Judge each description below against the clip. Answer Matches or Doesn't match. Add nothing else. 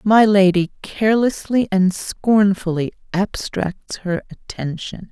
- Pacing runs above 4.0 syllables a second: Doesn't match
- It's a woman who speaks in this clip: Matches